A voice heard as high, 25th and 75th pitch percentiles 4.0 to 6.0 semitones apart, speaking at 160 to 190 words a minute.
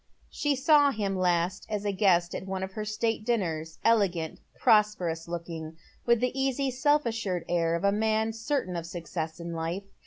Yes: high, 195 Hz; average, 5.0 semitones; average, 165 wpm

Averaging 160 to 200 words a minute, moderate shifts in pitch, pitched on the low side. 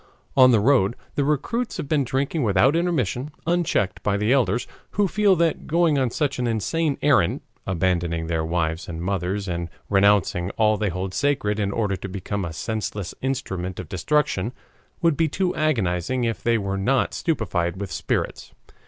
No: average, 170 wpm; wide, 7.4 semitones; low, 110 Hz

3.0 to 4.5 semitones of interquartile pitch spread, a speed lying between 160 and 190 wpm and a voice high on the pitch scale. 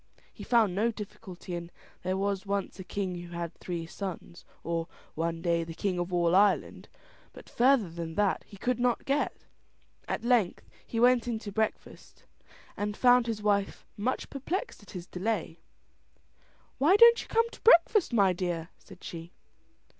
No: average, 5.2 semitones; average, 170 wpm; high, 200 Hz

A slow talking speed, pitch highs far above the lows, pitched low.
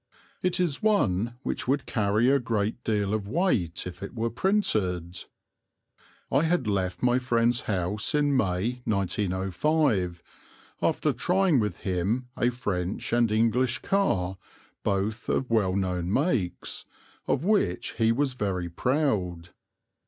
Yes: slow, 130 wpm; wide, 5.7 semitones; low, 110 Hz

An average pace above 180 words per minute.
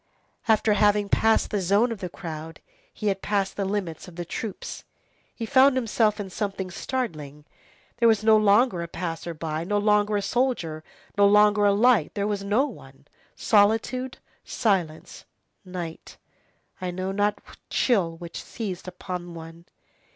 No: average, 160 wpm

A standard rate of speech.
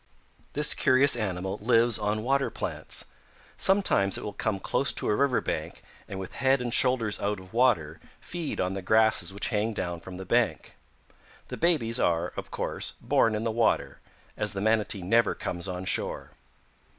Yes: average, 175 wpm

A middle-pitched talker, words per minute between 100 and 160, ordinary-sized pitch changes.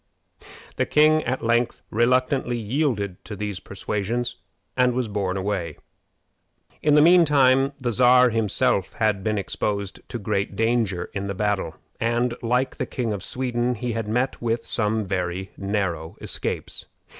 No: low, 115 Hz; average, 145 wpm; average, 3.8 semitones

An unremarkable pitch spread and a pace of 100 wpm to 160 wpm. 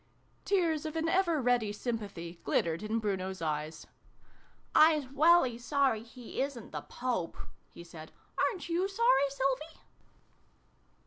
No: wide, 7.9 semitones; average, 140 wpm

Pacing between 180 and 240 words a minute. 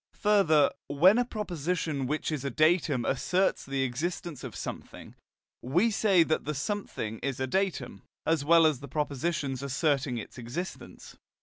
No: average, 150 wpm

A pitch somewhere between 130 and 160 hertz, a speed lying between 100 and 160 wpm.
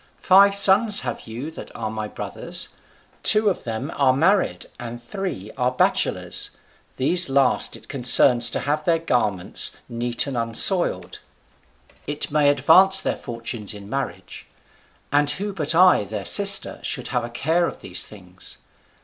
Yes: low, 135 Hz; average, 150 wpm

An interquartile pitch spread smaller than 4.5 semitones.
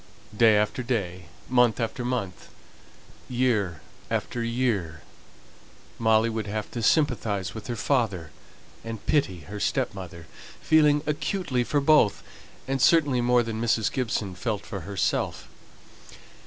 Yes: average, 4.0 semitones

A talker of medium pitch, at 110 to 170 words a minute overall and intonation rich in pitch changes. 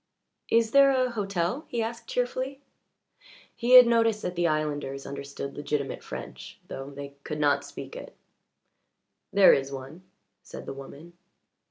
Yes: medium, 175 Hz; average, 145 wpm; wide, 8.8 semitones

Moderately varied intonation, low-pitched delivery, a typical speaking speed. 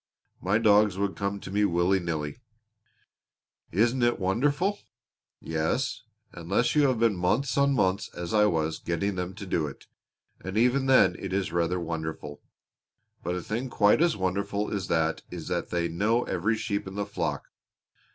Yes: average, 4.6 semitones; low, 100 Hz; average, 170 wpm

